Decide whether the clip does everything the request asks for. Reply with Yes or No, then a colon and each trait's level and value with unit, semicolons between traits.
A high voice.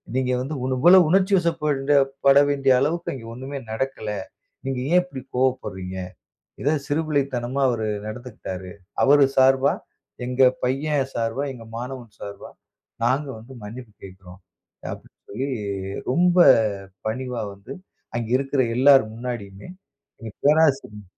No: low, 130 Hz